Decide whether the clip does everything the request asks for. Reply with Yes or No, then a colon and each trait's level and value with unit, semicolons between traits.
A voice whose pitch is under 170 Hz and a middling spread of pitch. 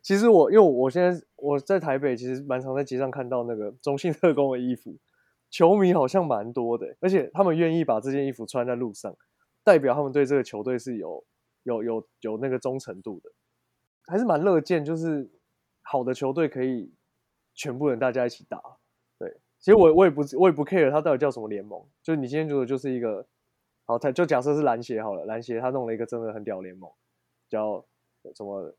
Yes: low, 135 Hz; average, 4.7 semitones